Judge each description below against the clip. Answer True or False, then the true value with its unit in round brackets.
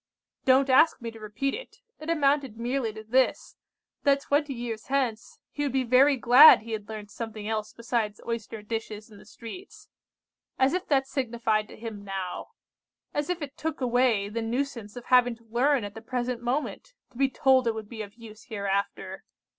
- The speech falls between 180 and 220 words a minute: True (195 wpm)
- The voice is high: True (235 Hz)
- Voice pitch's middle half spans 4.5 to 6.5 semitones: False (3.7 semitones)